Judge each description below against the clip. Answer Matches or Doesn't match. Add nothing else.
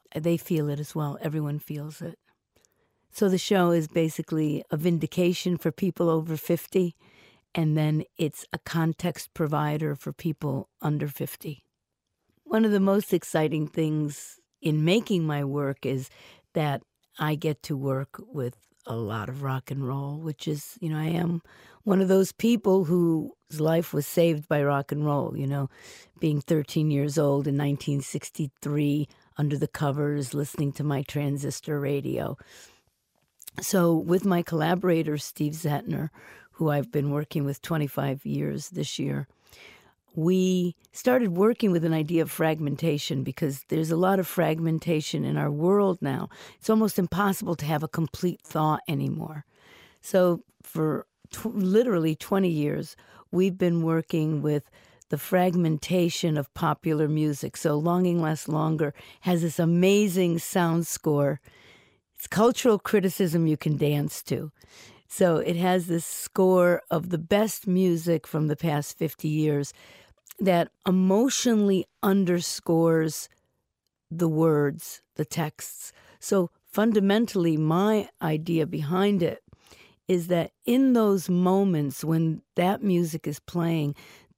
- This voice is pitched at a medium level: Matches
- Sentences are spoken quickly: Doesn't match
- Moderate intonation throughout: Matches